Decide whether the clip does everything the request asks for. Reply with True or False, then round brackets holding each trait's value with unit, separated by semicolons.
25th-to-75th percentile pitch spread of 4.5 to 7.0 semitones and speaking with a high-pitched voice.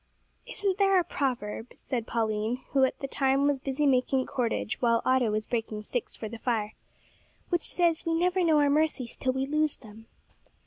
True (4.8 semitones; 260 Hz)